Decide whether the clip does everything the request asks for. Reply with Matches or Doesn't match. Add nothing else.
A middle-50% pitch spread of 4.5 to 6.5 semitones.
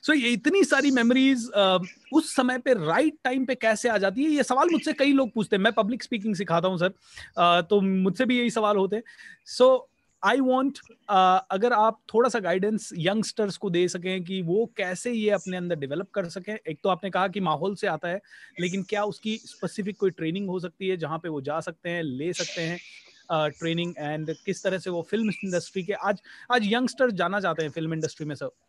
Matches